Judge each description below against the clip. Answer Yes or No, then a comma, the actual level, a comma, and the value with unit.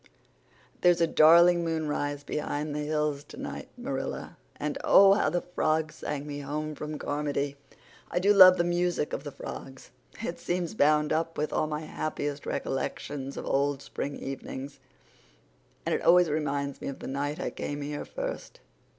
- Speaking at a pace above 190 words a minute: No, average, 165 wpm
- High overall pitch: No, medium, 150 Hz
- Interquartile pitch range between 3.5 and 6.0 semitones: No, average, 2.8 semitones